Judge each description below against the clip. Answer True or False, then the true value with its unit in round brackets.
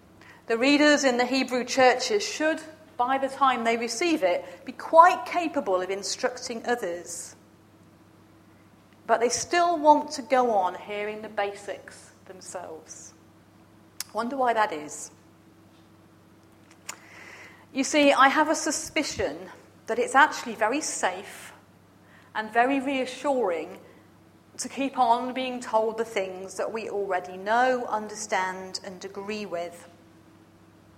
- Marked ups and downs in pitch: True (6.4 semitones)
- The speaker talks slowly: True (120 wpm)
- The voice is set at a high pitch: True (230 Hz)